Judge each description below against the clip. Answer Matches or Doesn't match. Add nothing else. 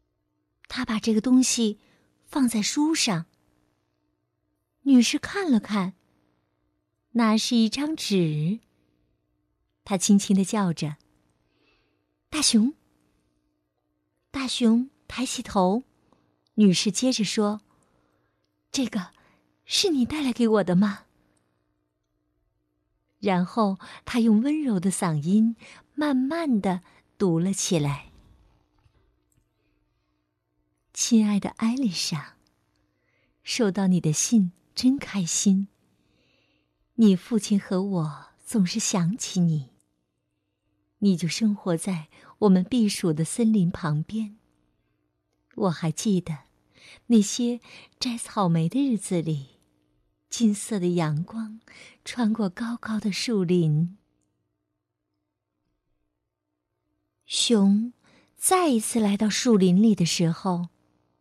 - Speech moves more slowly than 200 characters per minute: Matches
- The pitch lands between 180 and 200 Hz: Matches